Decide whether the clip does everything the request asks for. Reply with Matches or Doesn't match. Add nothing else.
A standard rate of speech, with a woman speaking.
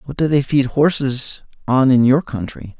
Doesn't match